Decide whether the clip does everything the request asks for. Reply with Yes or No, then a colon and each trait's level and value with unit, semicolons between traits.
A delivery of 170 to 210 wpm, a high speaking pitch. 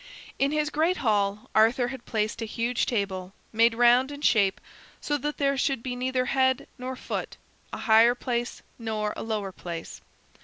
Yes: average, 175 wpm; high, 240 Hz